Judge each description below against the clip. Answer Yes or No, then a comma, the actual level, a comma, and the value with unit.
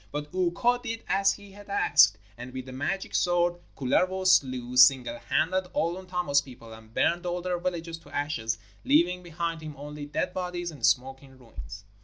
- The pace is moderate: Yes, average, 175 wpm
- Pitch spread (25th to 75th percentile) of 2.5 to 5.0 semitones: No, wide, 5.5 semitones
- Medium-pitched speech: Yes, medium, 165 Hz